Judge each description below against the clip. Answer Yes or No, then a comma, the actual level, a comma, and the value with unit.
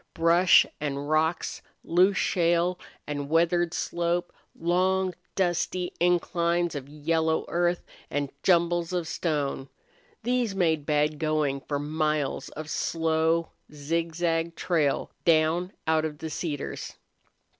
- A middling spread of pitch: No, narrow, 2.2 semitones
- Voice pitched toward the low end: No, medium, 165 Hz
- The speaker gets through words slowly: Yes, slow, 115 wpm